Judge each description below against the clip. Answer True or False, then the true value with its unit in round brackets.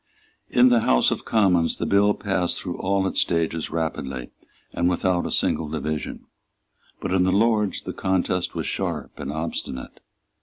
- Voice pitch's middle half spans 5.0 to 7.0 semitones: False (3.5 semitones)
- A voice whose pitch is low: True (90 Hz)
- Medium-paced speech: True (160 wpm)